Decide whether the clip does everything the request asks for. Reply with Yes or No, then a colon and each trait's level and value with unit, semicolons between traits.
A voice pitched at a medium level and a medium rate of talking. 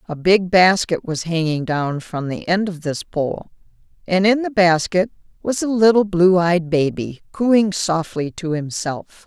Yes: medium, 175 Hz; average, 170 wpm